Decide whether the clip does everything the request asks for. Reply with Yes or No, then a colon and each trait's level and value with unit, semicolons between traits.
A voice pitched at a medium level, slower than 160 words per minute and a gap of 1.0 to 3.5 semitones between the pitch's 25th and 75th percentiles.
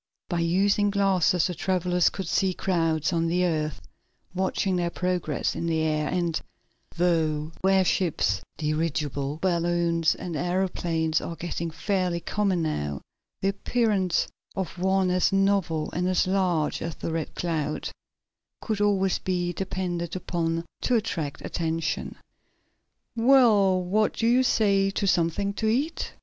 Yes: medium, 180 Hz; slow, 135 wpm; average, 2.9 semitones